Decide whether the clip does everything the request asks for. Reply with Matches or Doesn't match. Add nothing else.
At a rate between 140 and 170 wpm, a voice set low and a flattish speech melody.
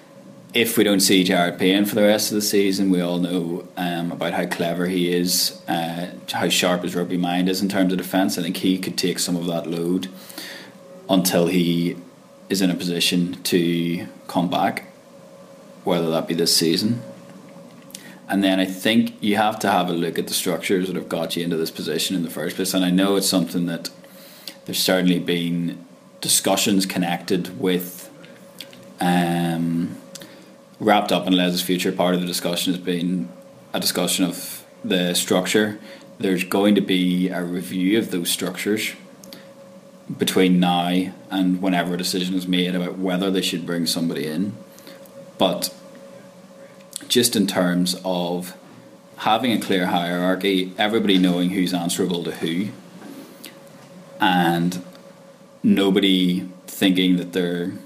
Matches